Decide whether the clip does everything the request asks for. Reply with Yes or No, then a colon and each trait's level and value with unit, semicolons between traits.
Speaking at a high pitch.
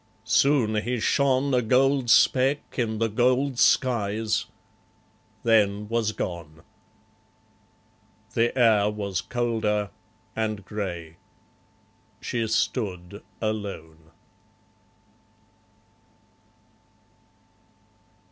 No: low, 110 Hz